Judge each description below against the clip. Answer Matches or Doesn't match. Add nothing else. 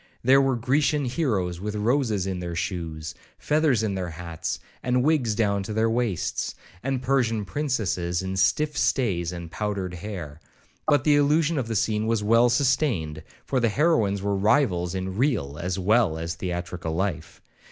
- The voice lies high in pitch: Doesn't match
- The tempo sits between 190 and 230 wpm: Doesn't match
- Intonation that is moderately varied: Doesn't match